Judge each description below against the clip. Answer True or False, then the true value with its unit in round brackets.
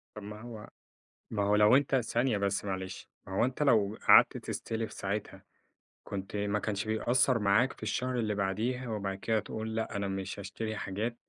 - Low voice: True (105 Hz)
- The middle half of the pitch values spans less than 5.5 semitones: True (2.5 semitones)